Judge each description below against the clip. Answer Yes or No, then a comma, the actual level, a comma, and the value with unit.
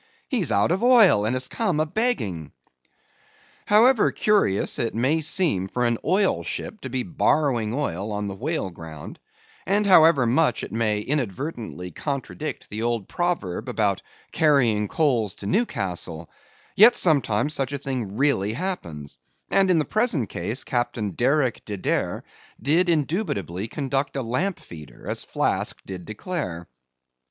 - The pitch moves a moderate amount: No, wide, 7.9 semitones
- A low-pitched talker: Yes, low, 130 Hz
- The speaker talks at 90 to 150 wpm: Yes, average, 145 wpm